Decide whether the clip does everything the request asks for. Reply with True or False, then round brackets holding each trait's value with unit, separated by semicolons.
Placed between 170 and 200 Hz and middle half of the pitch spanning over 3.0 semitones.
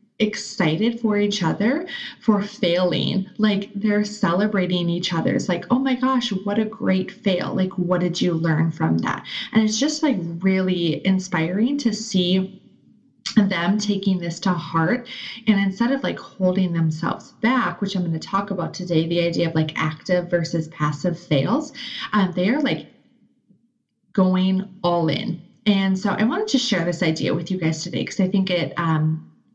True (190 Hz; 4.1 semitones)